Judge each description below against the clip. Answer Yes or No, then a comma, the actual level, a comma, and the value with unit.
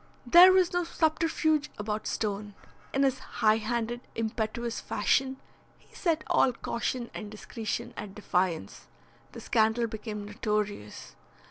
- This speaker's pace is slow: Yes, slow, 125 wpm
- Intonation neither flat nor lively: Yes, average, 4.0 semitones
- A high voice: Yes, high, 225 Hz